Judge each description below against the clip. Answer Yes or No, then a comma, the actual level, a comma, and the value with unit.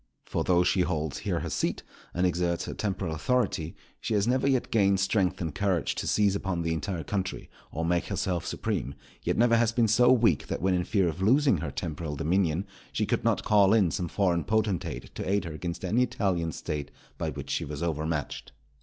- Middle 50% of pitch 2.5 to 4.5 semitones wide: Yes, average, 3.9 semitones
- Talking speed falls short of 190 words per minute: No, fast, 205 wpm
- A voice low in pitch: Yes, very low, 90 Hz